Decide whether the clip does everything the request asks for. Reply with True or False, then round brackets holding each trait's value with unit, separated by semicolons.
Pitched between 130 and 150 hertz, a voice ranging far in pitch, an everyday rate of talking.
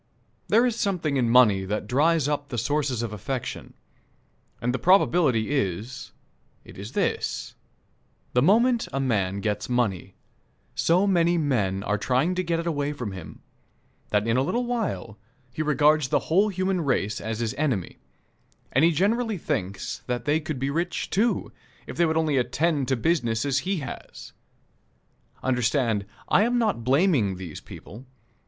True (135 Hz; 6.8 semitones; 160 wpm)